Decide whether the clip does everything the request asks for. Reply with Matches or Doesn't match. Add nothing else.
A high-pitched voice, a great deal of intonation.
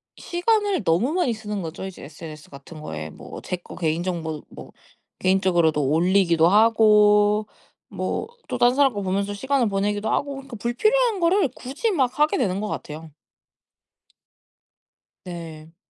Matches